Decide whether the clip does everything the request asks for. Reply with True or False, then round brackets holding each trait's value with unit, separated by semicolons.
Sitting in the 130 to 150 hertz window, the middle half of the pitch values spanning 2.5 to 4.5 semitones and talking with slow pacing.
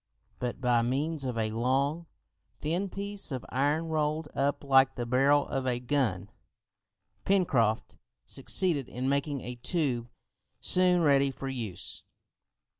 True (135 Hz; 3.8 semitones; 130 wpm)